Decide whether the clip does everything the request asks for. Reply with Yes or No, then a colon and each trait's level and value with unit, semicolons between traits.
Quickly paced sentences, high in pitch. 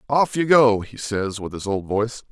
No: fast, 235 wpm; low, 115 Hz